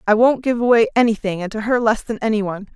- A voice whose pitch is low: No, high, 220 Hz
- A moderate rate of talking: No, fast, 260 wpm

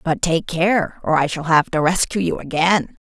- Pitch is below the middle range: No, medium, 170 Hz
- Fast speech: Yes, fast, 215 wpm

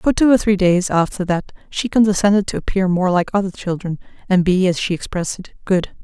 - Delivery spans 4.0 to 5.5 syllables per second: No, 5.8 syllables/s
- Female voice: Yes, female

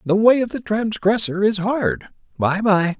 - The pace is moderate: Yes, average, 180 wpm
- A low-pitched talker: No, high, 205 Hz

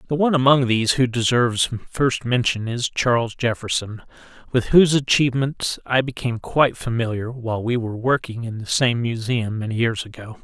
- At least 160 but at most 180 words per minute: Yes, average, 165 wpm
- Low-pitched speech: Yes, low, 120 Hz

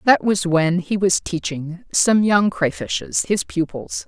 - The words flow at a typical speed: Yes, average, 160 wpm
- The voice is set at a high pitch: No, medium, 150 Hz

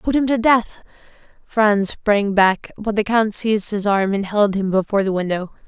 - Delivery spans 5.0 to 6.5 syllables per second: No, 4.7 syllables/s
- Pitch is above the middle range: Yes, high, 205 Hz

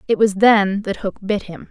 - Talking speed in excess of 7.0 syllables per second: No, 4.5 syllables/s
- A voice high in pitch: Yes, high, 205 Hz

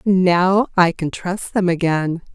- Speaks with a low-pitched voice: No, medium, 180 Hz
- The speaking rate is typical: Yes, average, 155 wpm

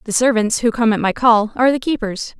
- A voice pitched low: No, high, 230 Hz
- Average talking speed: No, fast, 250 wpm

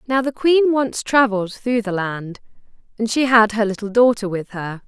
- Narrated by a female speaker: Yes, female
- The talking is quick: No, average, 195 wpm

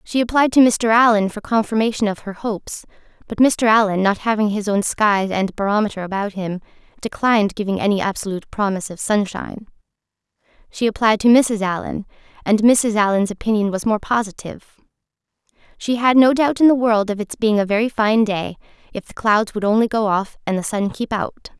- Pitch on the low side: No, high, 215 Hz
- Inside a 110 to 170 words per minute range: No, average, 185 wpm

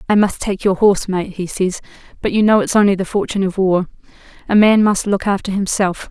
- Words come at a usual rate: No, fast, 225 wpm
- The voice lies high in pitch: Yes, high, 195 Hz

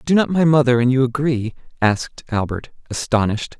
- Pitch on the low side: Yes, low, 130 Hz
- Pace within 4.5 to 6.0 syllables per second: Yes, 5.7 syllables/s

